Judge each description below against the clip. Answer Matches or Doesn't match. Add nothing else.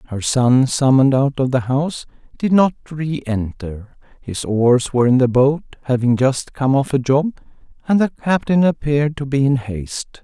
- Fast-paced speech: Doesn't match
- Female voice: Doesn't match